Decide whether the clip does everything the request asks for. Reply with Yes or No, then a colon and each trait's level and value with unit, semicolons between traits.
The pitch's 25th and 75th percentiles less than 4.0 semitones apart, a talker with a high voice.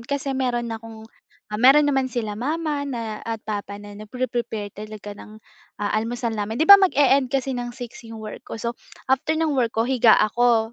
Yes: average, 3.5 semitones; high, 240 Hz